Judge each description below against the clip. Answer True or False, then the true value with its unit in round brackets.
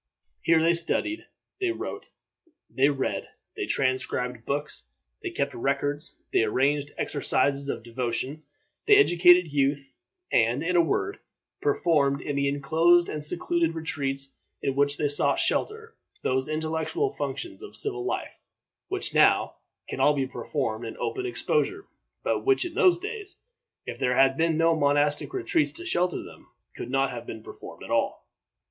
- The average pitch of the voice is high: False (150 Hz)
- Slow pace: False (155 wpm)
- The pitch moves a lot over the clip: False (4.9 semitones)